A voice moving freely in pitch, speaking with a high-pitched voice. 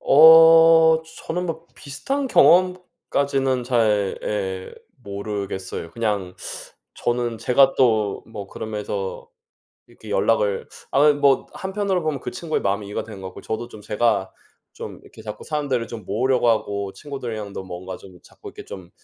No: wide, 6.6 semitones; low, 115 Hz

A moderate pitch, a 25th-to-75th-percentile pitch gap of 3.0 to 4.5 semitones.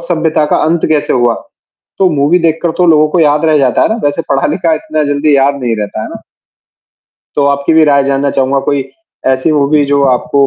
No: medium, 145 Hz; narrow, 2.5 semitones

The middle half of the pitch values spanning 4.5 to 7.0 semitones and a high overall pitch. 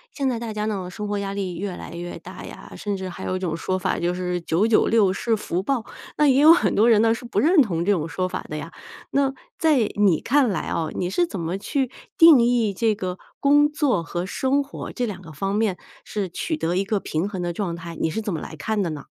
Yes: average, 5.0 semitones; high, 200 Hz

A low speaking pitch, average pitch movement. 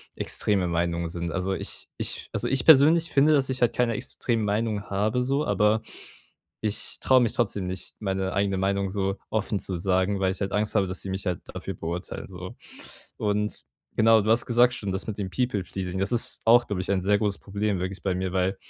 Yes: low, 100 Hz; average, 3.1 semitones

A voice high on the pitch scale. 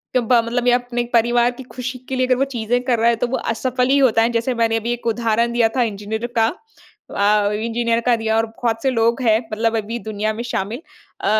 Yes: high, 235 Hz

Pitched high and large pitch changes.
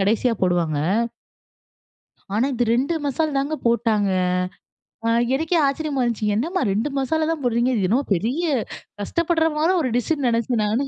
Yes: very high, 250 Hz; wide, 5.7 semitones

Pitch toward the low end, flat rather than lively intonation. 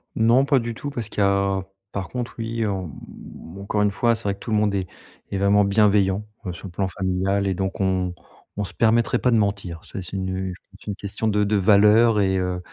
Yes: low, 100 Hz; narrow, 2.3 semitones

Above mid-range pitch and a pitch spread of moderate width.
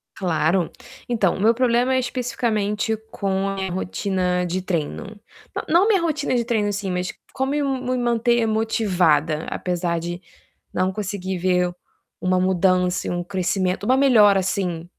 Yes: high, 195 Hz; average, 4.6 semitones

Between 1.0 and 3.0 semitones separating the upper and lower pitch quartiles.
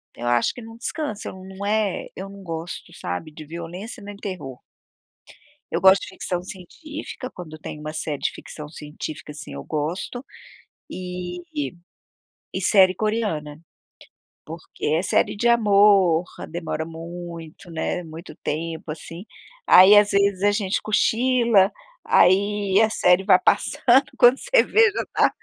No: average, 4.3 semitones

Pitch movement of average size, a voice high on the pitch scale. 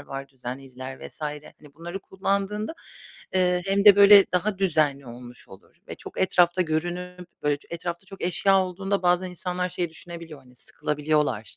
No: average, 4.3 semitones; medium, 175 Hz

